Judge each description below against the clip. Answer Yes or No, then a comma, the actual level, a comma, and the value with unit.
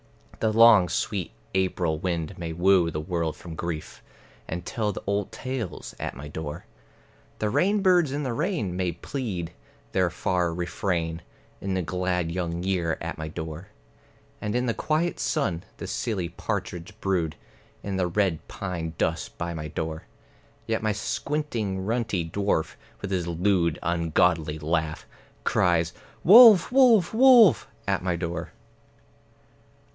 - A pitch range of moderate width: Yes, average, 4.6 semitones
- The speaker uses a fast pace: No, average, 140 wpm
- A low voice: Yes, very low, 90 Hz